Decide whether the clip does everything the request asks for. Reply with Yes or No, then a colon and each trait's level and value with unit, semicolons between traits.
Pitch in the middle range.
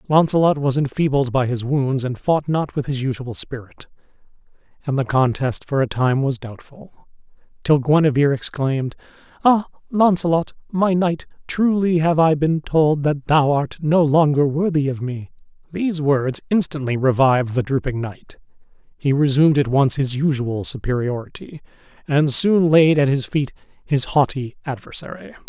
Yes: medium, 145 Hz